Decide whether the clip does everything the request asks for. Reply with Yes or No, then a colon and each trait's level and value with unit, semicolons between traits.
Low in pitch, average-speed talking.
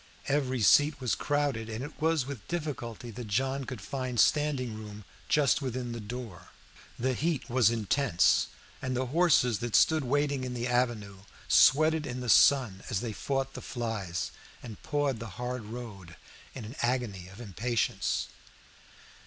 Yes: low, 125 Hz; average, 160 wpm